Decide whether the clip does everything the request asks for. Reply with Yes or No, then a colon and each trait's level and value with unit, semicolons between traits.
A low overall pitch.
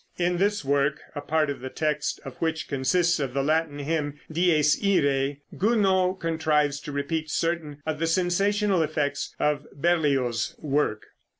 No: medium, 155 Hz